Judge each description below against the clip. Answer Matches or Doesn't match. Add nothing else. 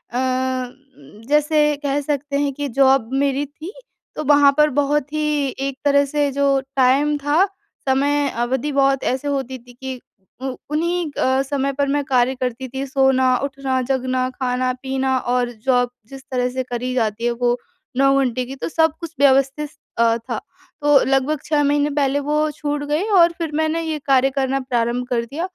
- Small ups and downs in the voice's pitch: Matches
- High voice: Matches